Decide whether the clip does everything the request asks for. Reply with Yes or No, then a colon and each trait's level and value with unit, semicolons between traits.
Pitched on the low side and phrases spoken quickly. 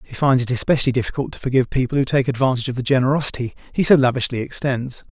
Yes: low, 130 Hz; fast, 210 wpm